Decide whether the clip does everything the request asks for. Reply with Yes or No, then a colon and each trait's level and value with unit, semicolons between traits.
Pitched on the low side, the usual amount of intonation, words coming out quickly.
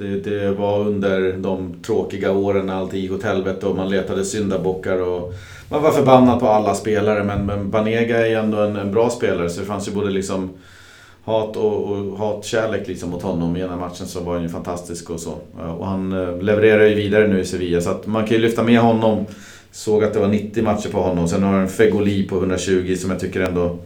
No: low, 100 Hz; narrow, 2.2 semitones; fast, 225 wpm